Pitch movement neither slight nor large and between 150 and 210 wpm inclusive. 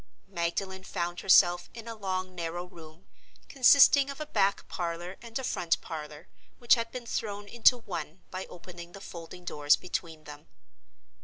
Yes: average, 4.5 semitones; average, 160 wpm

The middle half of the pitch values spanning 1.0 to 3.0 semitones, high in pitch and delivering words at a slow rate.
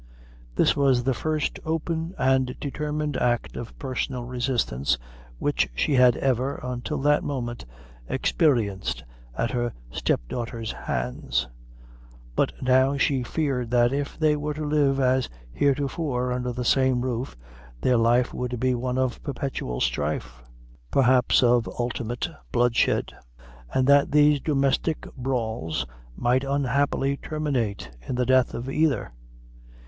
No: average, 2.7 semitones; low, 130 Hz; slow, 130 wpm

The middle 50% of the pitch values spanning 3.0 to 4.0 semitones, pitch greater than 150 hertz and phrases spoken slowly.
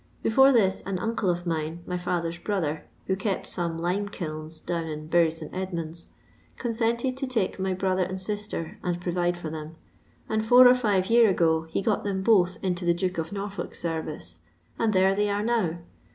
No: average, 3.7 semitones; medium, 185 Hz; average, 190 wpm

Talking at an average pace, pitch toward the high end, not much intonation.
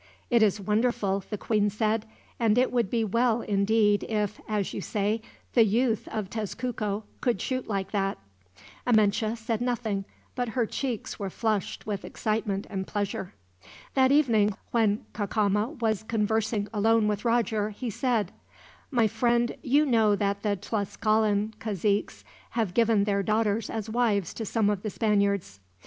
Yes: average, 155 wpm; high, 215 Hz; narrow, 2.1 semitones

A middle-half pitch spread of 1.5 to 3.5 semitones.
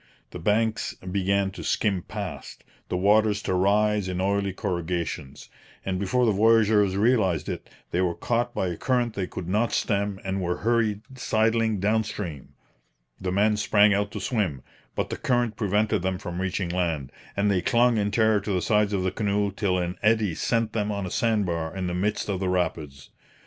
Yes: average, 2.9 semitones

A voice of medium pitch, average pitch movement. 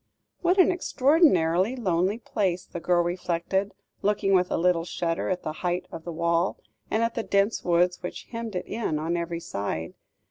Yes: medium, 180 Hz; average, 3.7 semitones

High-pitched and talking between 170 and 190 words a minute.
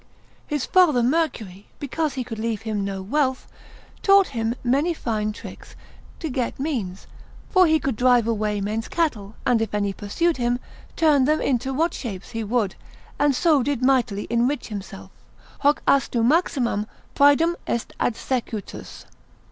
No: high, 245 Hz; average, 150 wpm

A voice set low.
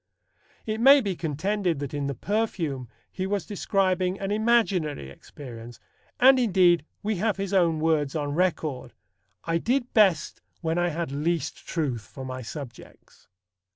No: medium, 170 Hz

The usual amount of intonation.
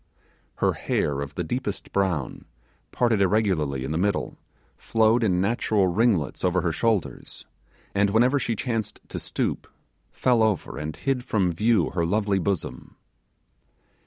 Yes: average, 4.6 semitones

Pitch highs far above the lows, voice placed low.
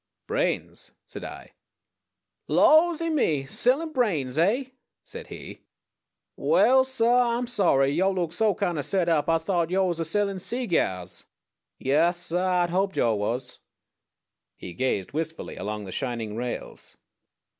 No: wide, 8.8 semitones; medium, 175 Hz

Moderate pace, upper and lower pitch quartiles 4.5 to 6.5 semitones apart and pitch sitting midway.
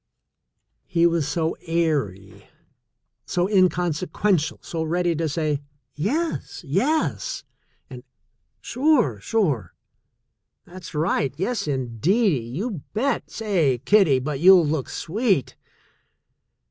No: slow, 95 wpm; wide, 5.4 semitones; medium, 170 Hz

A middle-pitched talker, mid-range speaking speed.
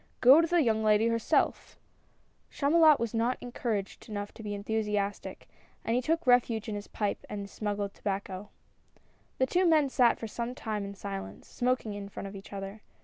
No: high, 220 Hz; average, 195 wpm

